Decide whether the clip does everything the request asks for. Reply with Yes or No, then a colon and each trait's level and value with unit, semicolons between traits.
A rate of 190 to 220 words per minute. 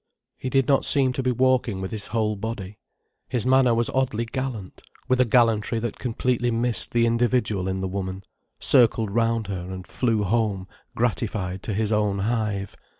No: average, 175 wpm